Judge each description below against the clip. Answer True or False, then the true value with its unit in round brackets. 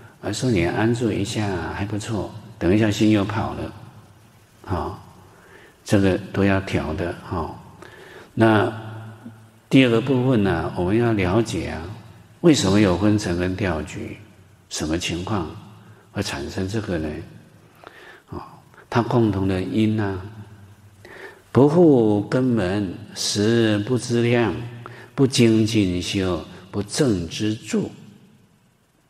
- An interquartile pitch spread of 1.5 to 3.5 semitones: True (2.8 semitones)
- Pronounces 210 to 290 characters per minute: False (175 characters per minute)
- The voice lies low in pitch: True (105 Hz)